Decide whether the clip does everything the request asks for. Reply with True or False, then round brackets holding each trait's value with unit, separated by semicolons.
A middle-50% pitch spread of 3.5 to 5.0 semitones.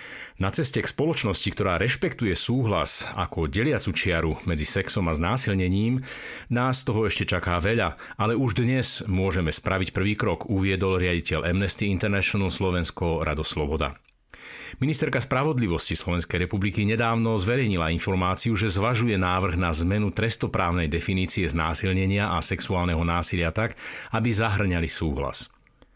True (4.3 semitones)